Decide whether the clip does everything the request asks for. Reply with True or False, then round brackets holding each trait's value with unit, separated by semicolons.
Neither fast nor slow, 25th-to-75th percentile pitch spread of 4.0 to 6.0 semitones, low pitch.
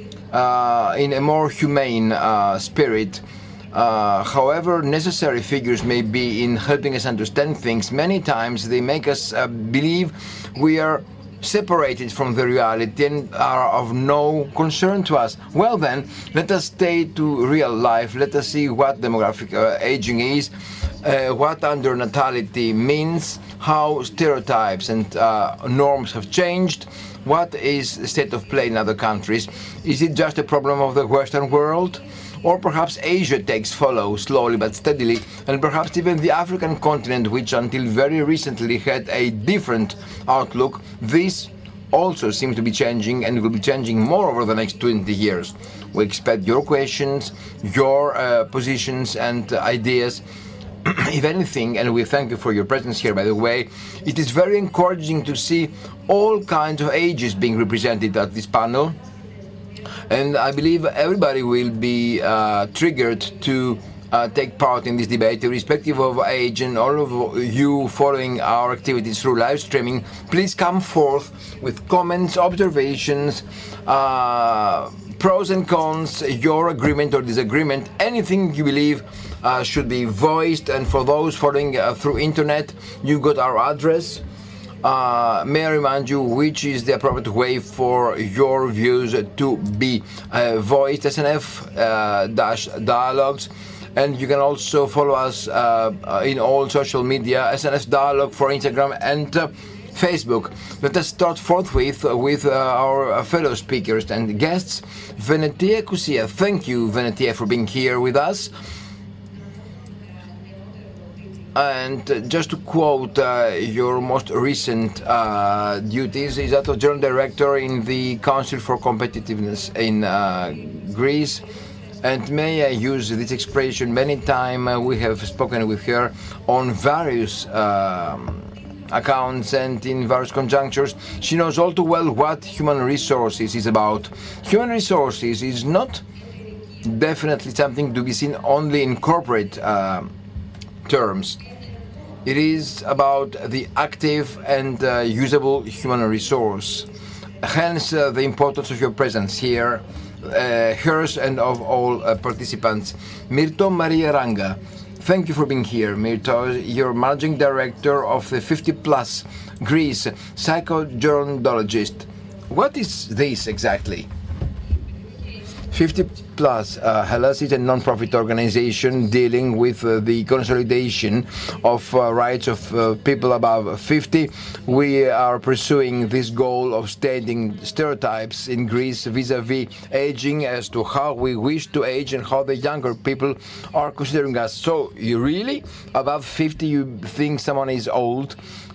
True (145 wpm; 4.9 semitones; 125 Hz)